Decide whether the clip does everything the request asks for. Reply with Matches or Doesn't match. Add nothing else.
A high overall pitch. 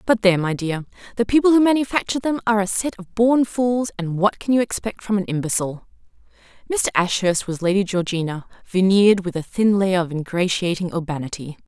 Matches